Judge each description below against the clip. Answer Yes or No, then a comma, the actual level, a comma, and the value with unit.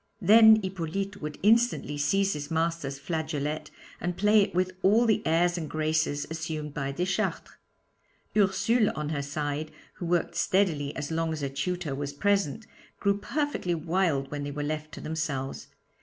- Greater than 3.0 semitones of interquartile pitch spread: Yes, average, 4.7 semitones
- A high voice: No, medium, 160 Hz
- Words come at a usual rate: Yes, average, 160 wpm